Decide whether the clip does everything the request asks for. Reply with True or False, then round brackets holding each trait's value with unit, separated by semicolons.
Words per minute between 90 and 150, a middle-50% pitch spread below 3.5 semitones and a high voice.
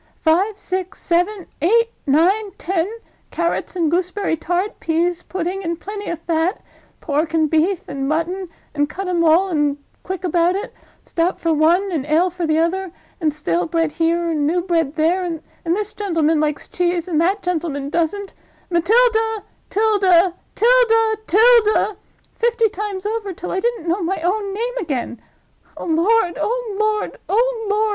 False (145 wpm; 3.9 semitones; 360 Hz)